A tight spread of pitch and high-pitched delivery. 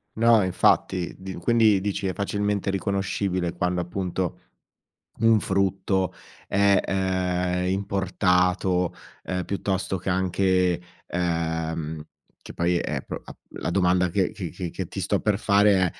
No: narrow, 1.7 semitones; very low, 95 Hz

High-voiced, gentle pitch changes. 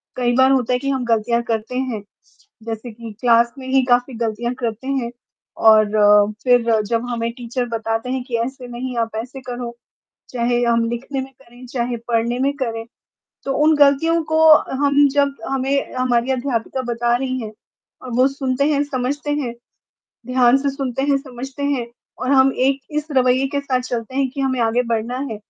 Yes: very high, 250 Hz; narrow, 2.3 semitones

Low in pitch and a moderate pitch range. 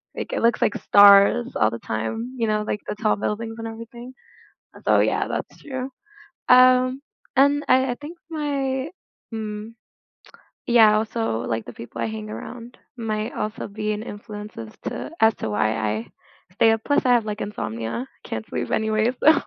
No: high, 220 Hz; average, 3.6 semitones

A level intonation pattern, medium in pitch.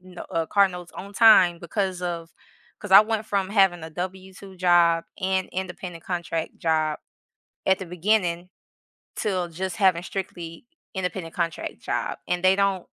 Yes: narrow, 2.0 semitones; medium, 180 Hz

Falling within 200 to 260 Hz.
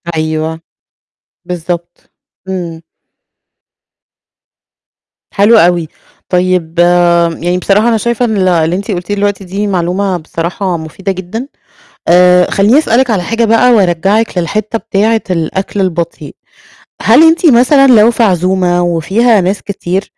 No: high, 190 Hz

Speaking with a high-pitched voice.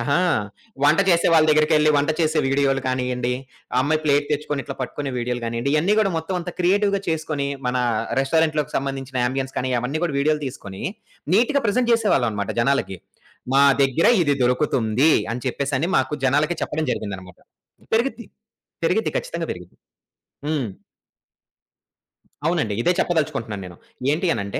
No: medium, 145 Hz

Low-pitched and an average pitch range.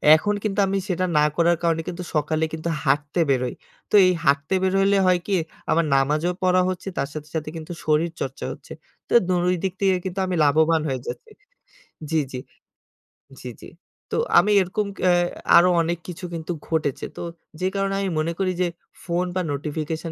No: medium, 170 Hz; average, 3.0 semitones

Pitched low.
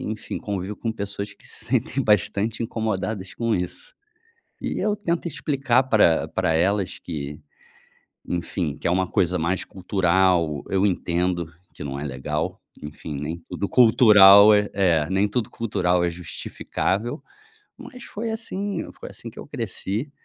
Yes: very low, 95 Hz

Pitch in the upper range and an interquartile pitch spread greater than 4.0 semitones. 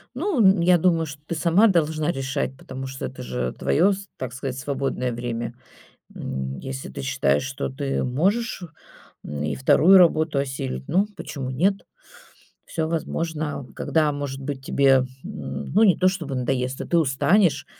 No: medium, 140 Hz; average, 4.9 semitones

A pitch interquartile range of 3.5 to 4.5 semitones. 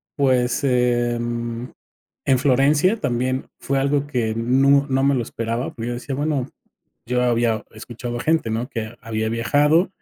No: average, 2.8 semitones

